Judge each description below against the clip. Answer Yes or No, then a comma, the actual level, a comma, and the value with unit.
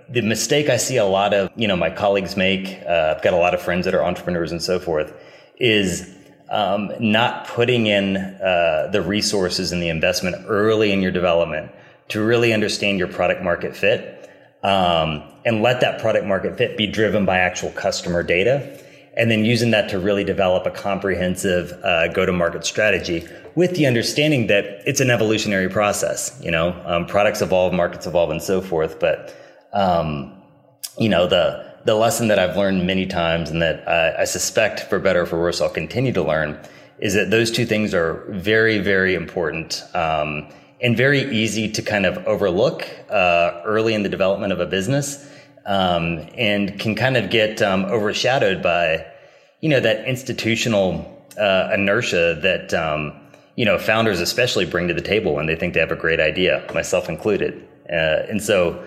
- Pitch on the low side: Yes, low, 100 Hz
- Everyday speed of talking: Yes, average, 180 wpm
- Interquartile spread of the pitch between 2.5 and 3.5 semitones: No, average, 3.9 semitones